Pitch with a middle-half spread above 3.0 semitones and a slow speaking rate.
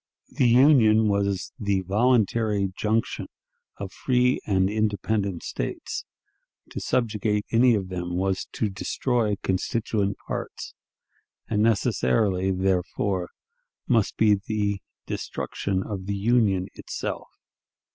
No: average, 2.7 semitones; slow, 105 wpm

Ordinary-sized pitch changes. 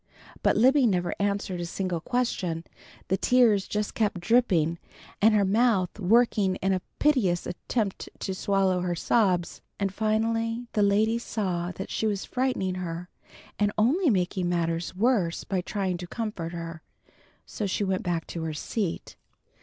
Yes: average, 3.8 semitones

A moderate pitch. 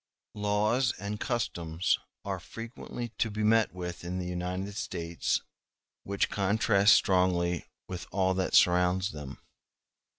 No: very low, 95 Hz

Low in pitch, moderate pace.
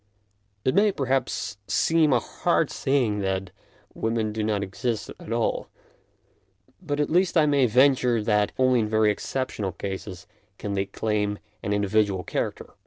Yes: low, 110 Hz; average, 150 wpm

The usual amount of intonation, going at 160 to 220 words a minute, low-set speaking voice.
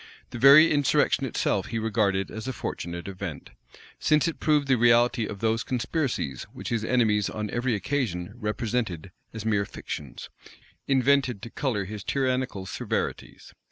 No: average, 4.6 semitones; average, 150 wpm; low, 115 Hz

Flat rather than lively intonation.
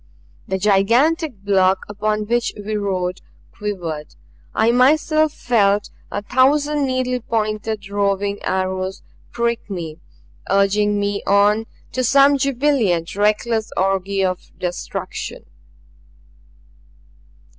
No: average, 3.7 semitones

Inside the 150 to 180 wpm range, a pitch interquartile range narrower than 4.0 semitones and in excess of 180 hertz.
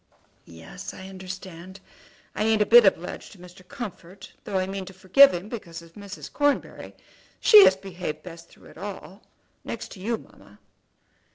Yes: average, 170 wpm; average, 2.9 semitones; high, 190 Hz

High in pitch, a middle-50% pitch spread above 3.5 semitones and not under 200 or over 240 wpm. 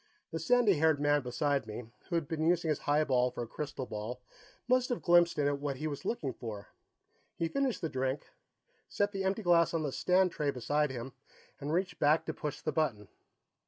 No: medium, 150 Hz; average, 4.5 semitones; fast, 205 wpm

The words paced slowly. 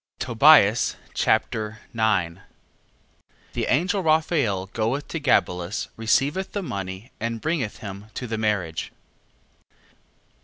Yes: slow, 105 wpm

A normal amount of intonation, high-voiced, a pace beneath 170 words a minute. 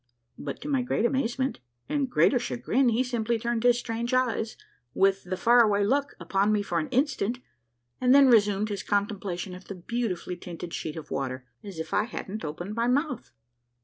No: average, 4.4 semitones; high, 220 Hz; average, 190 wpm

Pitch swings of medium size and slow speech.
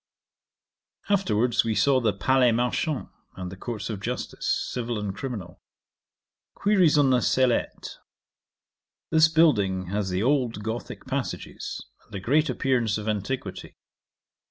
Yes: average, 4.4 semitones; slow, 130 wpm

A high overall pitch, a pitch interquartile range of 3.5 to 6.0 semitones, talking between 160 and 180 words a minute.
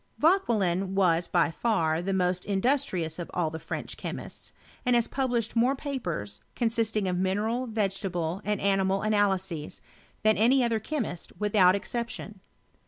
No: high, 200 Hz; average, 4.3 semitones; average, 140 wpm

